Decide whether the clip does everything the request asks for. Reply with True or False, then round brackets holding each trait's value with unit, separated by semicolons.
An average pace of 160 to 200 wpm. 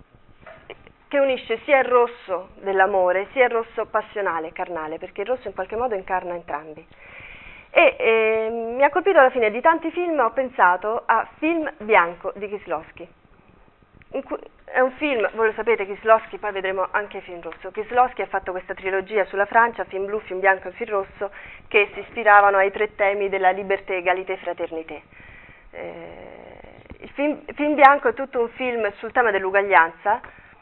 True (165 wpm)